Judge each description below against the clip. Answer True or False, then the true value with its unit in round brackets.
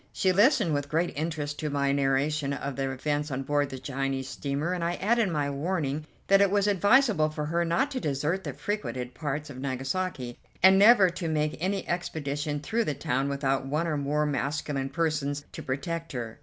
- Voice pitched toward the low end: False (150 Hz)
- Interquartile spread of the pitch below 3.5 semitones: False (4.1 semitones)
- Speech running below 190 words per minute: False (195 wpm)